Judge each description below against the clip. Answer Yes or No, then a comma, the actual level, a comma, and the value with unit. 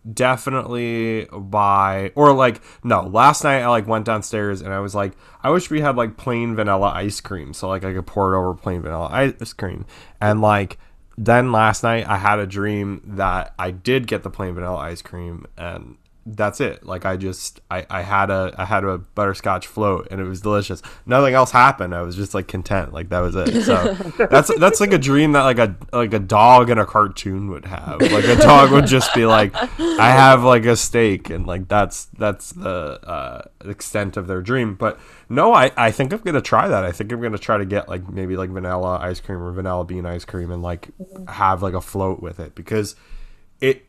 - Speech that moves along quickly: Yes, fast, 220 wpm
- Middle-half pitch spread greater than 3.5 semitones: Yes, average, 3.9 semitones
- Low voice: Yes, low, 100 Hz